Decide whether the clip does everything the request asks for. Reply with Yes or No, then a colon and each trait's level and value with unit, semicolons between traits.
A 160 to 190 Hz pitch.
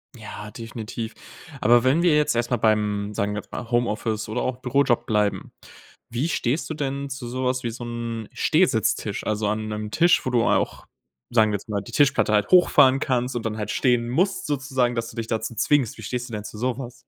No: low, 120 Hz